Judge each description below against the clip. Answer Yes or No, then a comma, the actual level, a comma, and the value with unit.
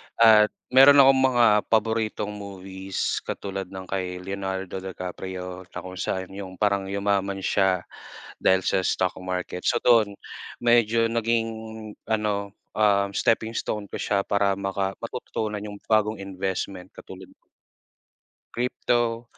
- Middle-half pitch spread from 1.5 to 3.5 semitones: Yes, average, 2.8 semitones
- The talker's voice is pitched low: Yes, low, 100 Hz